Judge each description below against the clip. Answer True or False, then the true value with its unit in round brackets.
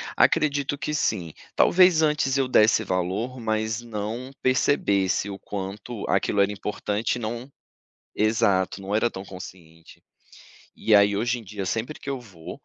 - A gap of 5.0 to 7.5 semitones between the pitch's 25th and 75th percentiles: False (4.4 semitones)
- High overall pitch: False (110 Hz)